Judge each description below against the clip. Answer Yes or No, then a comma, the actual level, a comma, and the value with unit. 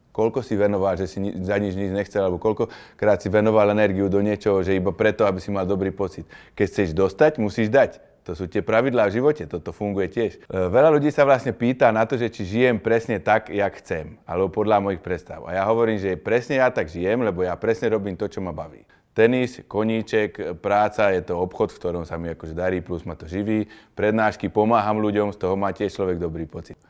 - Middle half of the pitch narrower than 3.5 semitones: Yes, narrow, 2.5 semitones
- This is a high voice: No, low, 100 Hz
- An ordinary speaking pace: No, fast, 220 wpm